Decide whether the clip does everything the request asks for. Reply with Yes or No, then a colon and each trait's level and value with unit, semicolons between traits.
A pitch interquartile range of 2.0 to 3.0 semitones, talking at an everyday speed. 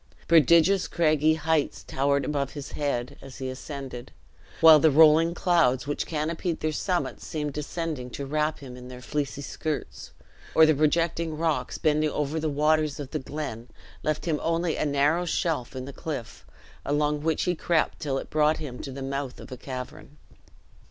Yes: narrow, 2.5 semitones; average, 175 wpm